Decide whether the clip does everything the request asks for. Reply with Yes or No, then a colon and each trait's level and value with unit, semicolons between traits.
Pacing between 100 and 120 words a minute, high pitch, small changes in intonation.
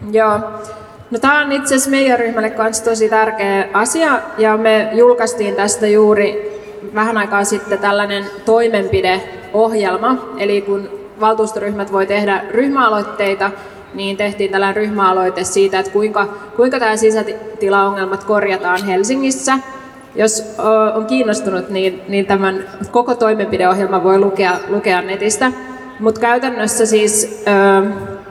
Yes: average, 115 wpm; high, 210 Hz; narrow, 1.9 semitones